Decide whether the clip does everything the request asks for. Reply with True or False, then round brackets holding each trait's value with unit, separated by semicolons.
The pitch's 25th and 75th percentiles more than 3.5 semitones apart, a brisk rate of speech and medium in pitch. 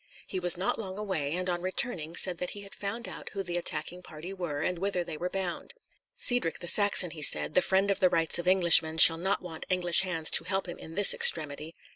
False (2.8 semitones; 235 wpm; 180 Hz)